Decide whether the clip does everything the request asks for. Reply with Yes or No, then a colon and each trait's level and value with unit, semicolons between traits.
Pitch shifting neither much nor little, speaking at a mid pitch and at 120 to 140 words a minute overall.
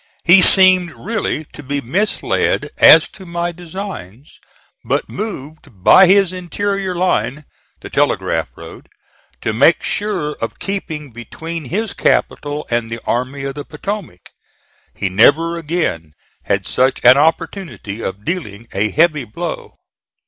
No: wide, 6.5 semitones; medium, 155 Hz; slow, 135 wpm